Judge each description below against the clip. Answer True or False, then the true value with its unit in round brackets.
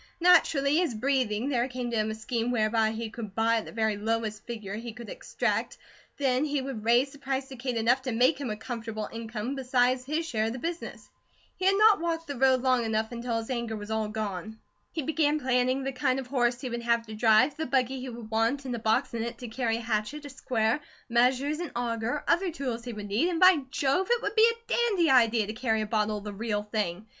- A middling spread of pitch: True (3.6 semitones)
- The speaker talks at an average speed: False (240 wpm)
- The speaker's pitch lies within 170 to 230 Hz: False (240 Hz)